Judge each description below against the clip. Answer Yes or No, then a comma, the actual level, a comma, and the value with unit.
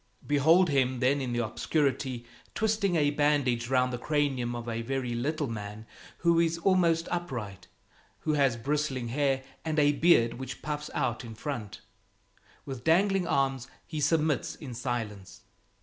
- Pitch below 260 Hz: Yes, low, 135 Hz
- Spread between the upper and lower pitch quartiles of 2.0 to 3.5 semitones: No, average, 4.2 semitones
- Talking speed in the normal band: Yes, average, 150 wpm